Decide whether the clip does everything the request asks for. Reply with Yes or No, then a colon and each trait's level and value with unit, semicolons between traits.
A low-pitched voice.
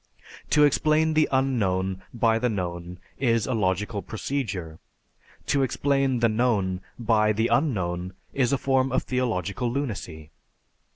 Yes: low, 115 Hz